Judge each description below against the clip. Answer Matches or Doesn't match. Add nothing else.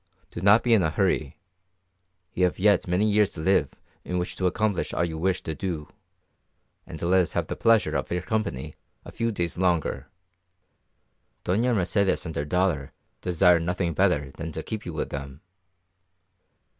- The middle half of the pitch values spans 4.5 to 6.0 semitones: Doesn't match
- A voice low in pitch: Matches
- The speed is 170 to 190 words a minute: Matches